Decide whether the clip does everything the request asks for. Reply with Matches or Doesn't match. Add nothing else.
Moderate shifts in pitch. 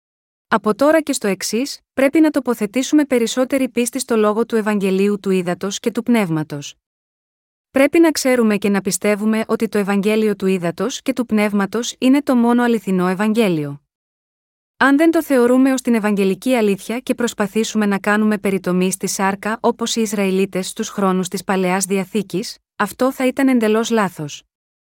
Matches